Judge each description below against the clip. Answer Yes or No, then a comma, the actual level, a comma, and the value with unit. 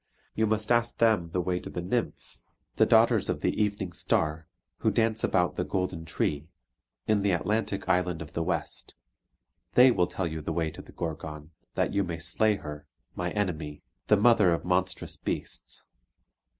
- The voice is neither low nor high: No, very low, 90 Hz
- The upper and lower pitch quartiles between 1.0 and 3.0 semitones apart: No, average, 4.2 semitones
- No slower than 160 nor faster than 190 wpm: Yes, average, 175 wpm